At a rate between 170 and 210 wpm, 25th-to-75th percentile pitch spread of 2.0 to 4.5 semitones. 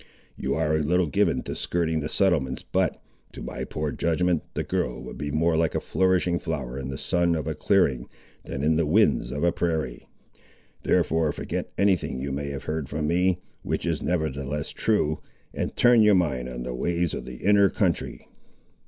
Yes: average, 195 wpm; average, 3.9 semitones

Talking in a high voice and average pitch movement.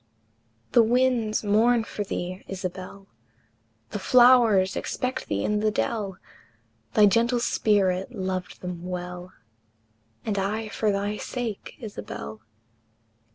Yes: high, 205 Hz; average, 3.5 semitones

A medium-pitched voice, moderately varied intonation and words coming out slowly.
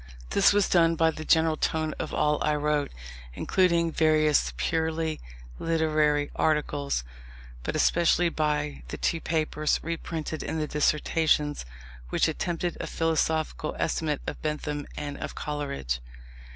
No: medium, 155 Hz; narrow, 1.6 semitones; slow, 130 wpm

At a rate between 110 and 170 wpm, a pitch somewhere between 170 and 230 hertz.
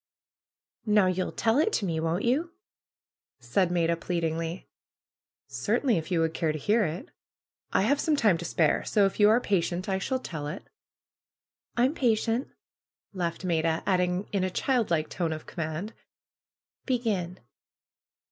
Yes: average, 155 wpm; medium, 185 Hz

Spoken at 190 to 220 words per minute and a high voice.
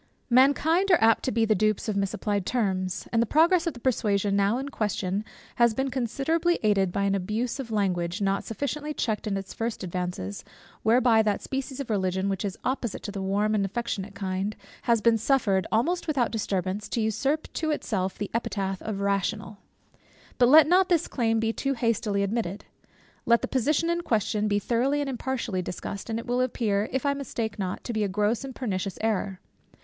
Yes: average, 195 wpm; high, 220 Hz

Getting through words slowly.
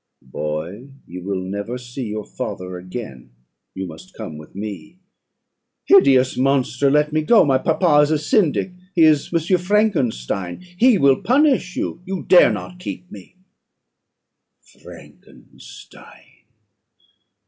Yes: slow, 125 wpm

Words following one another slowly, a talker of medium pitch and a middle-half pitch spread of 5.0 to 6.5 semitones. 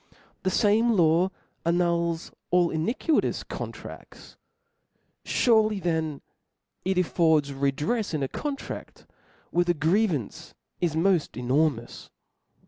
No: slow, 105 wpm; medium, 170 Hz; average, 3.8 semitones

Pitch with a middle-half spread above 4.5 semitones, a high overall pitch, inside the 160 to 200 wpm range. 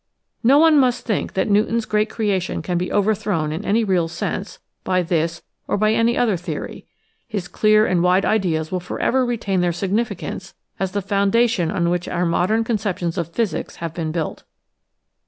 No: average, 3.9 semitones; high, 195 Hz; average, 180 wpm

